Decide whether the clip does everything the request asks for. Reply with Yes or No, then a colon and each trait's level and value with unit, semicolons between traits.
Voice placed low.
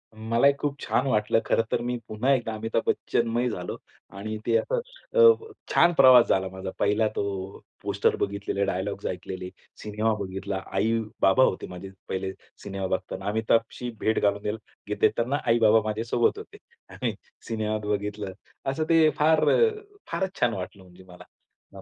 Yes: low, 110 Hz